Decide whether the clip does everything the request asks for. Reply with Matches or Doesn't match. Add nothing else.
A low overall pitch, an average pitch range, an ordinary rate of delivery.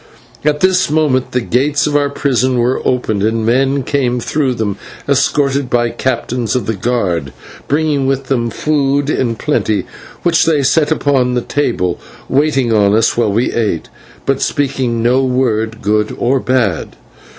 Matches